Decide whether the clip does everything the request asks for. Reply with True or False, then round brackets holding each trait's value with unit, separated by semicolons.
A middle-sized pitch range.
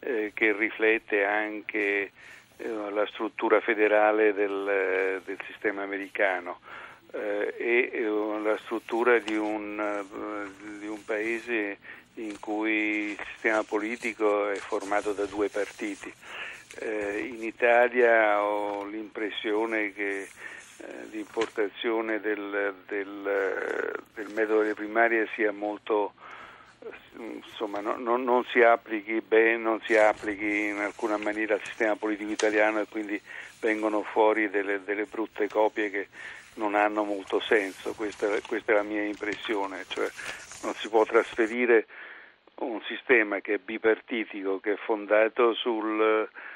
False (1.3 semitones)